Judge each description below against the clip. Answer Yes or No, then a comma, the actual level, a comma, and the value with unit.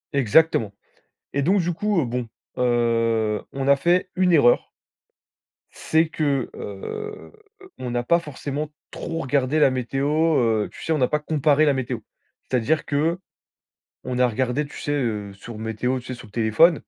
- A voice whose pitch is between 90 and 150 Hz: Yes, low, 135 Hz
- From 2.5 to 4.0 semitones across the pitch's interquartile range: No, average, 4.5 semitones